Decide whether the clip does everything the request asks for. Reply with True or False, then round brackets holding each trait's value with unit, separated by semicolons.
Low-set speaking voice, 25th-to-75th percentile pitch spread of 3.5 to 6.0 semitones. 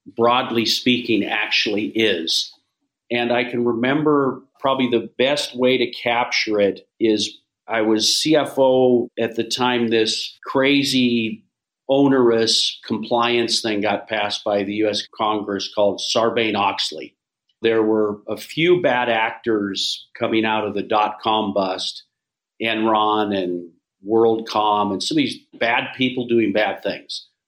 False (115 Hz; 2.7 semitones)